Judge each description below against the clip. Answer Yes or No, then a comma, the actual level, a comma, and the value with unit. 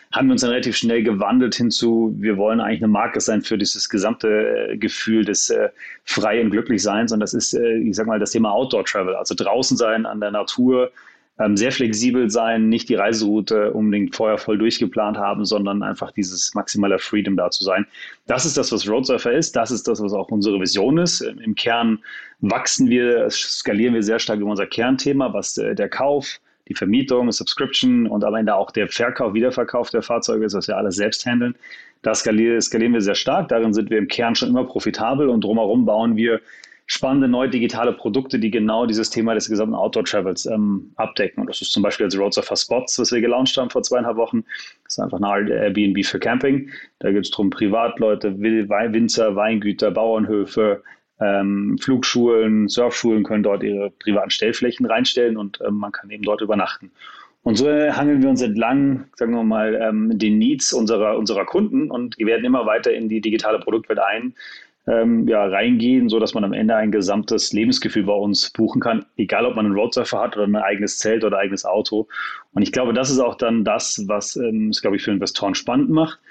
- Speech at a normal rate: No, fast, 195 wpm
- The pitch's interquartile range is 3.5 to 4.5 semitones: No, narrow, 2.6 semitones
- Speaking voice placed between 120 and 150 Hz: No, low, 110 Hz